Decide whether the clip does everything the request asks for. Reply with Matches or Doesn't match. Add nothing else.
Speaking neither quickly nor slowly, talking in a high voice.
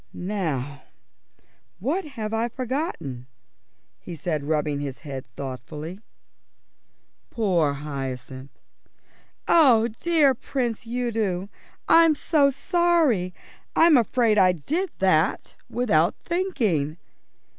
Doesn't match